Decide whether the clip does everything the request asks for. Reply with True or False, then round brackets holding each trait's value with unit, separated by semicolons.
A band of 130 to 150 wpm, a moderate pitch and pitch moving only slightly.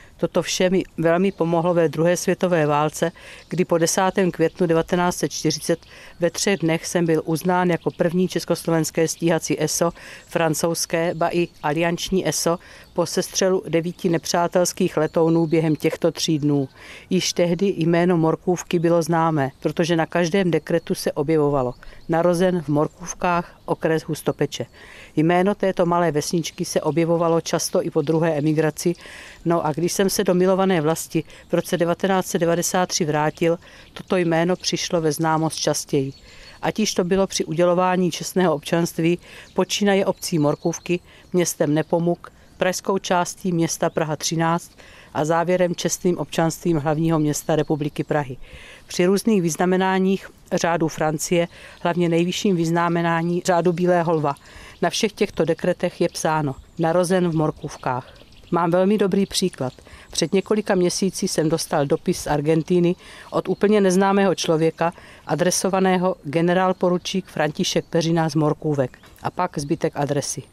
True (135 wpm; 170 Hz; 2.1 semitones)